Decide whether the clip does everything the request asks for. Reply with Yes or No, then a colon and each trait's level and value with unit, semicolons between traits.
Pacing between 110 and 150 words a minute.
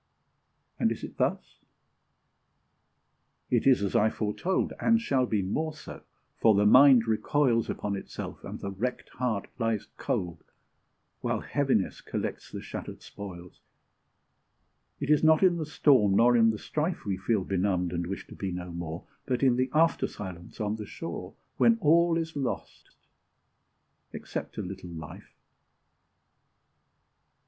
Yes: average, 145 wpm